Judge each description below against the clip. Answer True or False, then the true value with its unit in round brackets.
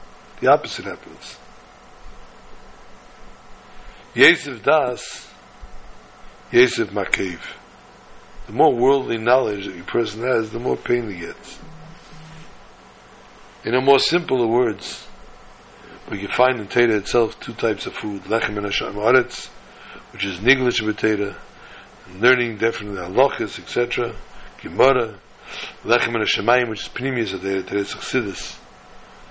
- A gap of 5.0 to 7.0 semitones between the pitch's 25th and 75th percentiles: False (4.3 semitones)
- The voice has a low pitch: True (115 Hz)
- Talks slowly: True (120 wpm)